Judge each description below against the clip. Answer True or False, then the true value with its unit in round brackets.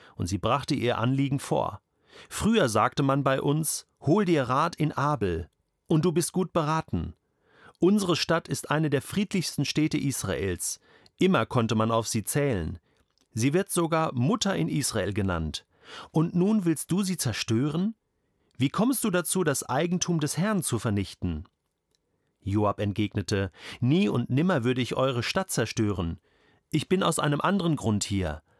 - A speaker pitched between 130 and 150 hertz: True (135 Hz)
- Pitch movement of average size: False (8.0 semitones)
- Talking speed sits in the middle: True (155 wpm)